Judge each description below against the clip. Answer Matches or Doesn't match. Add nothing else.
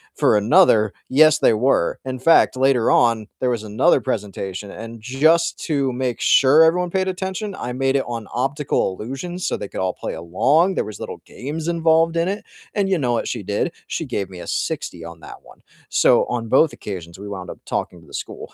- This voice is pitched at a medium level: Doesn't match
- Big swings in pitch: Matches